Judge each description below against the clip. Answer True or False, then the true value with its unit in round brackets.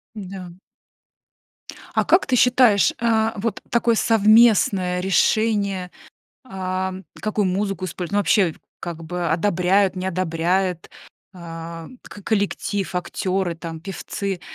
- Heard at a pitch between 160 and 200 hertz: True (190 Hz)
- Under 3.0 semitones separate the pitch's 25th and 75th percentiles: True (2.6 semitones)